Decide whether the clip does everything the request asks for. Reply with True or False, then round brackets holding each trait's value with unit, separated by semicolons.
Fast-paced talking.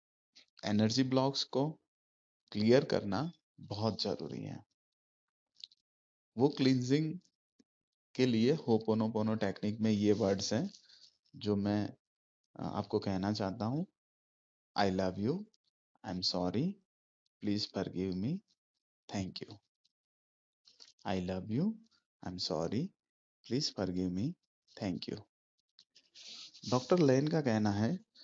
False (115 wpm)